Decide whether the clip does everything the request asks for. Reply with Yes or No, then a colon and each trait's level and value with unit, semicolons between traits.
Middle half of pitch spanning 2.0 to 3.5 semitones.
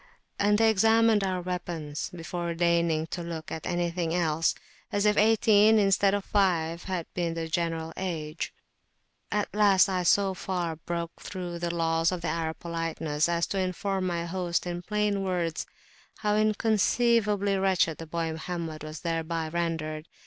Yes: average, 3.0 semitones